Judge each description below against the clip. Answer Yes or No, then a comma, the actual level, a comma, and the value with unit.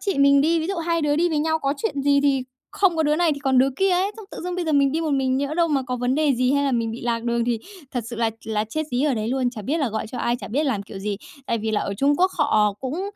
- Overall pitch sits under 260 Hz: No, very high, 275 Hz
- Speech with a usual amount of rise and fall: Yes, average, 4.8 semitones